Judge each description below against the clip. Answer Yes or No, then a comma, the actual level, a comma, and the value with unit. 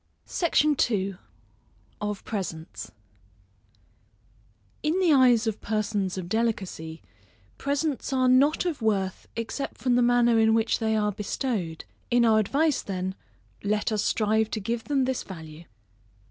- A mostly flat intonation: No, average, 4.4 semitones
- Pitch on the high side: Yes, high, 220 Hz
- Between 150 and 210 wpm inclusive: No, slow, 135 wpm